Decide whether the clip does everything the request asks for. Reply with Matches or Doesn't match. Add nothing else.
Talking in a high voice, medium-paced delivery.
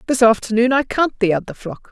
Doesn't match